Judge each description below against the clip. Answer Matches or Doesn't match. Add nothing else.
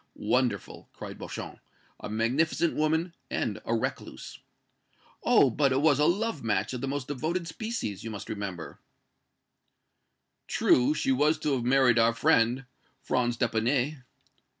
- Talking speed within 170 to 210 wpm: Doesn't match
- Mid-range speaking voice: Doesn't match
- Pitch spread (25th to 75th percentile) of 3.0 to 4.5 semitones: Doesn't match